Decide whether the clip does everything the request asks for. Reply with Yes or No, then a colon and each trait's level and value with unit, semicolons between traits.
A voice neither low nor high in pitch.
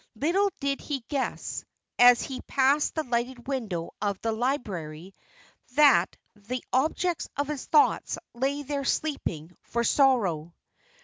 No: very high, 255 Hz